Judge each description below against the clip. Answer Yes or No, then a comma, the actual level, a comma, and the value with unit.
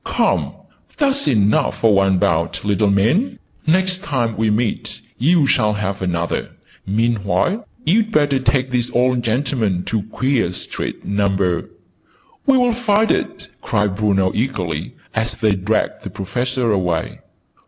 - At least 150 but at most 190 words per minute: No, slow, 135 wpm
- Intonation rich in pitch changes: Yes, wide, 5.8 semitones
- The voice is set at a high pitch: No, low, 110 Hz